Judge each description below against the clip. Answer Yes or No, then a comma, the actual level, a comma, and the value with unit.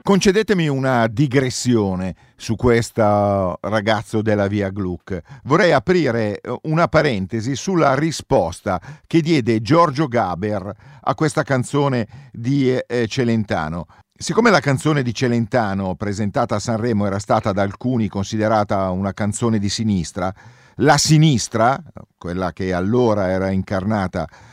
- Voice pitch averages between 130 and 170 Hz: No, low, 115 Hz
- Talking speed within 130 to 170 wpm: No, slow, 115 wpm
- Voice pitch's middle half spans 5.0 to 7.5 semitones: Yes, wide, 5.6 semitones